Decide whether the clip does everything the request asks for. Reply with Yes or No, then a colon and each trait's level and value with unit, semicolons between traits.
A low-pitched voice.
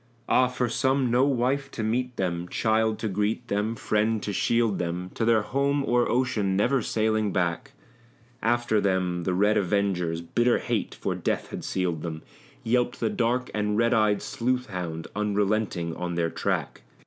Yes: low, 110 Hz